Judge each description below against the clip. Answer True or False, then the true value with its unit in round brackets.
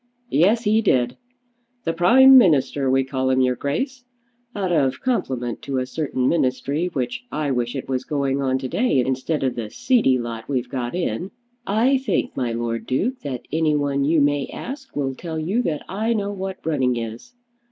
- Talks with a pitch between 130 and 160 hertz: True (140 Hz)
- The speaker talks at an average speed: True (185 wpm)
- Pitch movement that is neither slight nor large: False (6.6 semitones)